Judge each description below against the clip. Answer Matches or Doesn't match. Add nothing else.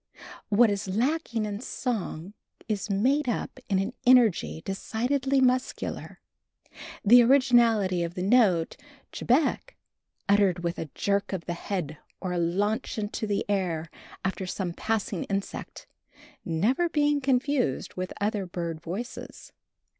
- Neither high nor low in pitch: Doesn't match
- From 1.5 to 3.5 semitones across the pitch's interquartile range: Doesn't match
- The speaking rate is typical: Doesn't match